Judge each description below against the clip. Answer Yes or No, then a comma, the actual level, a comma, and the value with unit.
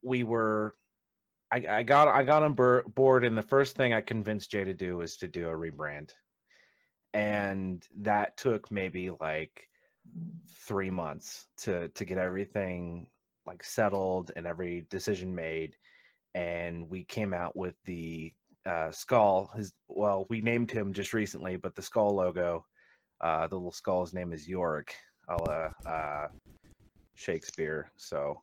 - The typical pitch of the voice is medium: No, very low, 95 Hz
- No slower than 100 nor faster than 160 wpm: Yes, average, 150 wpm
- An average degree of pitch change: Yes, average, 3.9 semitones